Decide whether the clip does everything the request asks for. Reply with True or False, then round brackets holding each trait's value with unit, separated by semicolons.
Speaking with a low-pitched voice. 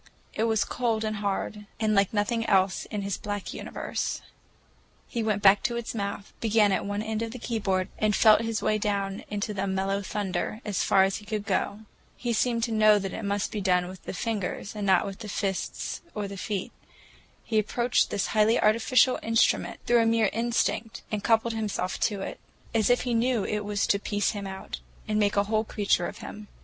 False (210 Hz)